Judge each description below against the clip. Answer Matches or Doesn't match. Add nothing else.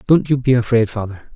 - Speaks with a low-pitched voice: Matches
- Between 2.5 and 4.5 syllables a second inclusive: Doesn't match